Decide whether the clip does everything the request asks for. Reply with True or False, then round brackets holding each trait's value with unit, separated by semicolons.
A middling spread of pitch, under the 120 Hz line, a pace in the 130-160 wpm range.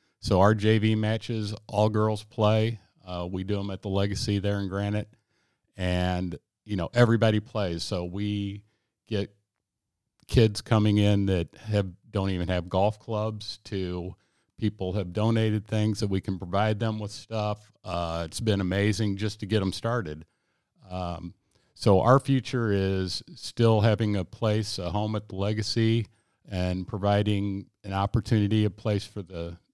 False (2.2 semitones; 105 Hz; 155 wpm)